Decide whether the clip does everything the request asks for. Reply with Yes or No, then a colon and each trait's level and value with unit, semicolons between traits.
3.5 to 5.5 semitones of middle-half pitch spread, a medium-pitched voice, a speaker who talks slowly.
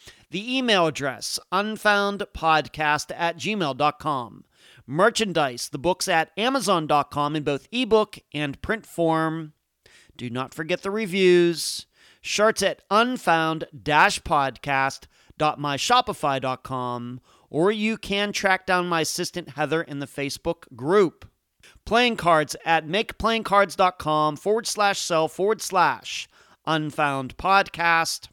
Yes: average, 5.2 semitones; medium, 165 Hz; slow, 100 wpm